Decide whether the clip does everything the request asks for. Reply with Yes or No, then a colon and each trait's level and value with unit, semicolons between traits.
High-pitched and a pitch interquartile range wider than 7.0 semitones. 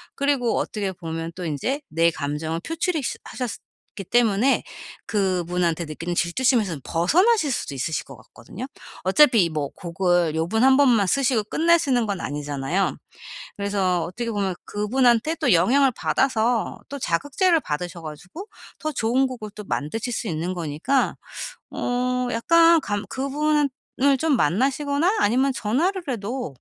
Yes: high, 220 Hz; wide, 7.8 semitones